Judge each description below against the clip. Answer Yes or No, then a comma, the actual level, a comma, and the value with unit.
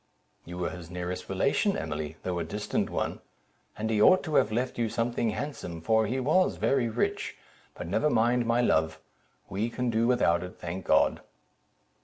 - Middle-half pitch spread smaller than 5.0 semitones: No, wide, 5.6 semitones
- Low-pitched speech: Yes, low, 110 Hz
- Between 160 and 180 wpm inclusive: Yes, average, 175 wpm